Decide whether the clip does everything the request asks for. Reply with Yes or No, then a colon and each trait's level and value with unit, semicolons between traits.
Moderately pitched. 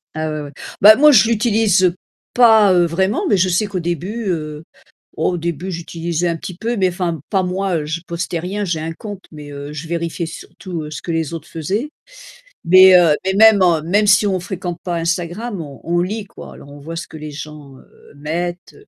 Yes: medium, 175 Hz